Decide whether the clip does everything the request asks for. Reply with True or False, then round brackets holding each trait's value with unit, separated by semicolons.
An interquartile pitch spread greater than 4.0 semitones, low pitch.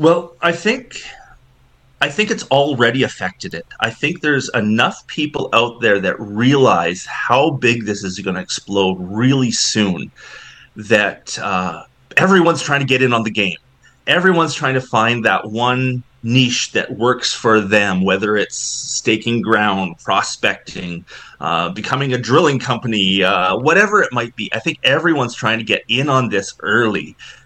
True (4.4 semitones; 120 Hz)